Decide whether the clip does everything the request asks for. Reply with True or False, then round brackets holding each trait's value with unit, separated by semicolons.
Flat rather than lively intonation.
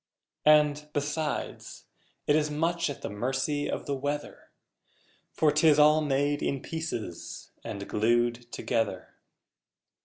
False (3.8 semitones)